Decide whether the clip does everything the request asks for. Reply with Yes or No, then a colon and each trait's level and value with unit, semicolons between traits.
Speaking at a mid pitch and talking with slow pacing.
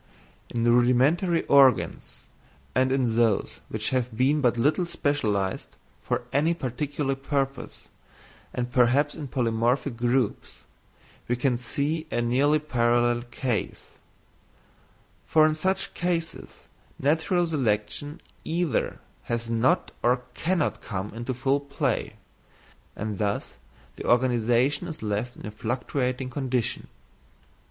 No: low, 130 Hz; slow, 115 wpm